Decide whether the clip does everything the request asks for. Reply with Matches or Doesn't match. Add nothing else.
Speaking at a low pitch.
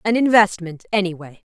Doesn't match